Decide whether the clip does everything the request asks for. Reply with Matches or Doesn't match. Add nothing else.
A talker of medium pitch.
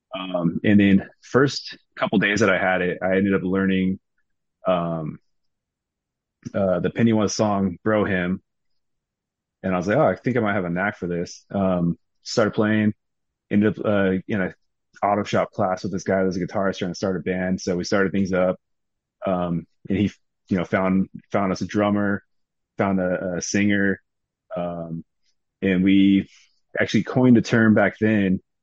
Doesn't match